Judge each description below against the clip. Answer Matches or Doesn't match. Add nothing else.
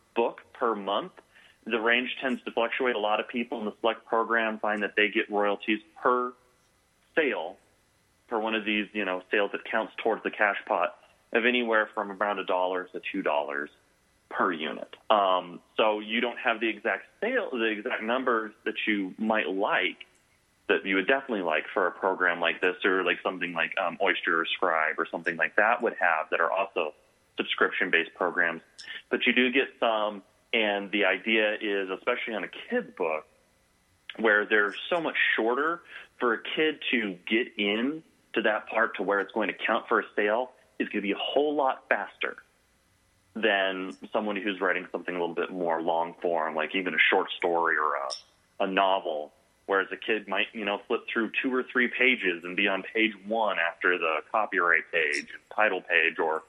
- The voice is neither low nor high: Doesn't match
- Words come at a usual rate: Matches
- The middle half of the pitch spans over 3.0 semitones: Matches